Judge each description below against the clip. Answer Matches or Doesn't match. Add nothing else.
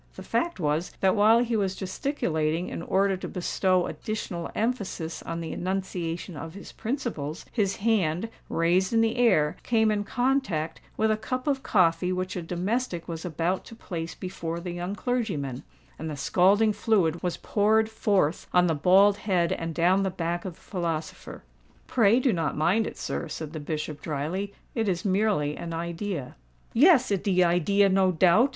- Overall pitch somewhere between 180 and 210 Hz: Matches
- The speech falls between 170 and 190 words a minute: Matches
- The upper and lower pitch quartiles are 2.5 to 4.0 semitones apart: Doesn't match